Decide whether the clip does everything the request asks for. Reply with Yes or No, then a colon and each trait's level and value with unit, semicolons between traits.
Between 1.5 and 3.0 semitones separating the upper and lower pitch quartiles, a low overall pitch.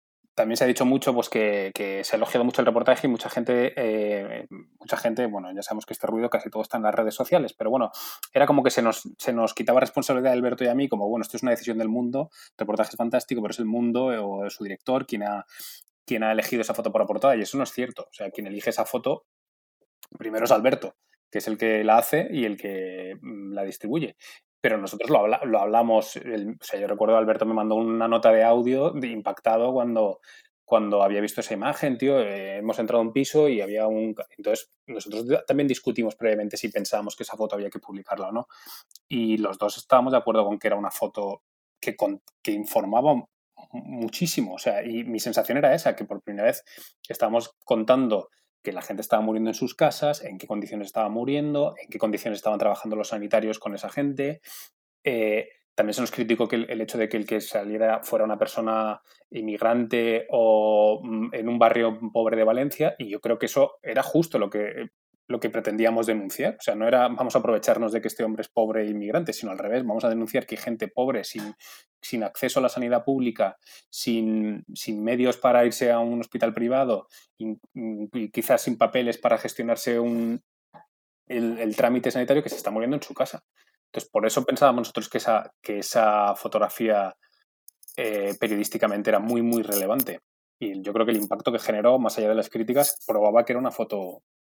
Yes: narrow, 2.6 semitones; low, 115 Hz